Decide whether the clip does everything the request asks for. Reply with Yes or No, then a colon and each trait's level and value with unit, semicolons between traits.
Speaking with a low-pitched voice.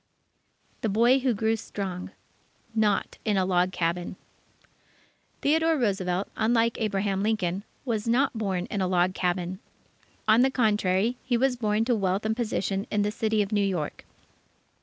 No: high, 210 Hz